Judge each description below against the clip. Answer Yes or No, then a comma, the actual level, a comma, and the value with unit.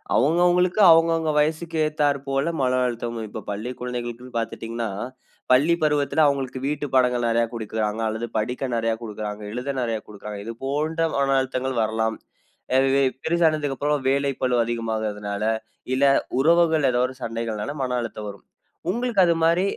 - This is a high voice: No, low, 130 Hz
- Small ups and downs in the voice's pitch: No, average, 4.7 semitones